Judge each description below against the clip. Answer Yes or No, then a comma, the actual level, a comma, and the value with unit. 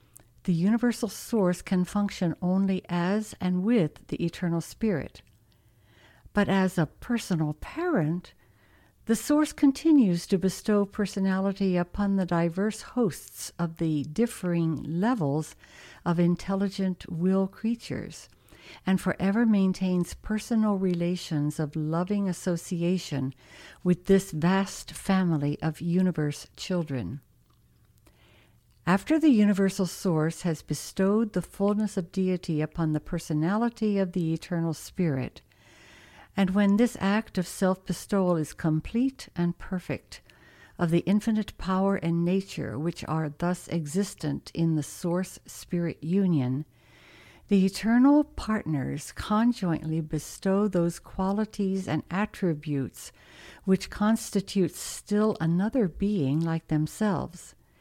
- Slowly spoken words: Yes, slow, 115 wpm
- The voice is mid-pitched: Yes, medium, 180 Hz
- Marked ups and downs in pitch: No, average, 4.1 semitones